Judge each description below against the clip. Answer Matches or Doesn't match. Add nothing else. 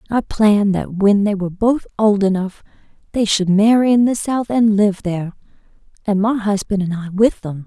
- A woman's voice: Matches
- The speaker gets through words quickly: Doesn't match